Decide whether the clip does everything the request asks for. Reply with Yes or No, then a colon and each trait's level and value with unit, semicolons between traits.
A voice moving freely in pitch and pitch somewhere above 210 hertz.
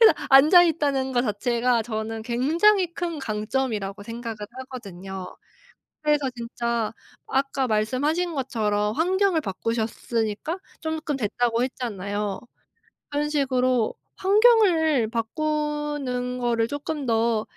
No: average, 5.0 semitones; very high, 250 Hz